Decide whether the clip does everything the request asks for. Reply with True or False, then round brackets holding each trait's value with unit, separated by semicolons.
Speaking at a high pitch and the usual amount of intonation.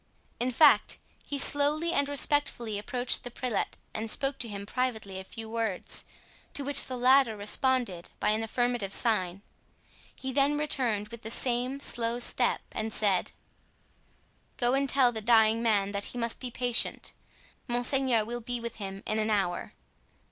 True (235 Hz; 3.3 semitones)